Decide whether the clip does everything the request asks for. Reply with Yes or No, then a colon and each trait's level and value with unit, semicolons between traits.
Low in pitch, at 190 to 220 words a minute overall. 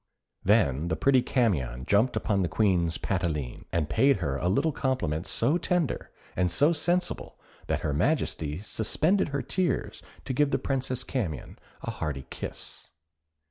No: low, 105 Hz; average, 150 wpm